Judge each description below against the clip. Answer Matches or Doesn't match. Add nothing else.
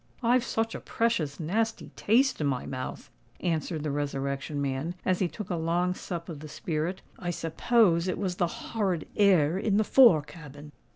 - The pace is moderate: Matches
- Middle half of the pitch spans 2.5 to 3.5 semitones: Doesn't match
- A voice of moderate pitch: Matches